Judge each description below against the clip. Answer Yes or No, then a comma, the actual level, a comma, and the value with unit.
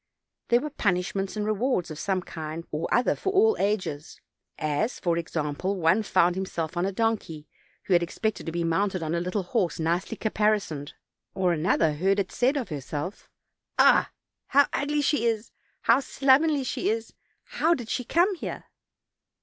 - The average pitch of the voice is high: Yes, high, 195 Hz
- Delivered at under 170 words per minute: No, average, 175 wpm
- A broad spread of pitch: Yes, wide, 5.8 semitones